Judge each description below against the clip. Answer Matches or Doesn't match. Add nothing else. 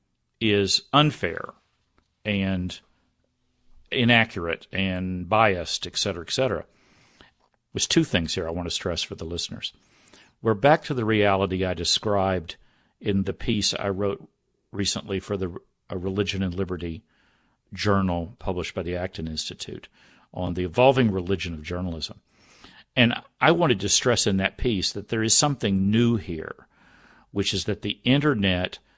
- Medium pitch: Doesn't match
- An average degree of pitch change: Matches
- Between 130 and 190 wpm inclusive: Matches